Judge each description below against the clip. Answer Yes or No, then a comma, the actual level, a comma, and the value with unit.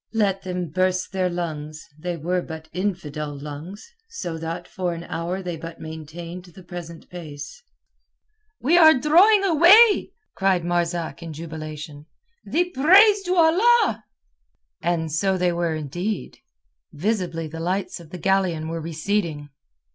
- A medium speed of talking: No, slow, 130 wpm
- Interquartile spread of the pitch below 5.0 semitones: Yes, average, 3.9 semitones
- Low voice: No, medium, 175 Hz